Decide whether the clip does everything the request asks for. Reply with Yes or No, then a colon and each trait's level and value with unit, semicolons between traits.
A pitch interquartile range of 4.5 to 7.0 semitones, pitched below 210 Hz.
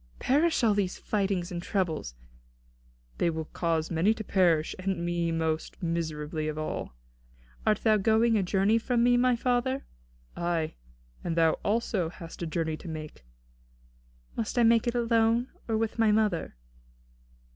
Yes: wide, 5.5 semitones; high, 190 Hz